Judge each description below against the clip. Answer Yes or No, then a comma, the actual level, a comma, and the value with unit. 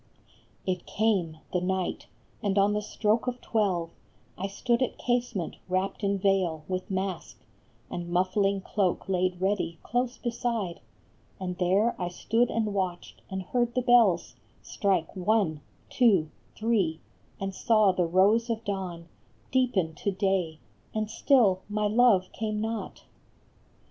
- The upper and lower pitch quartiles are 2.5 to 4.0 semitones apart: Yes, average, 3.4 semitones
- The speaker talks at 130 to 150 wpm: Yes, average, 140 wpm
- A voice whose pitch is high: Yes, high, 195 Hz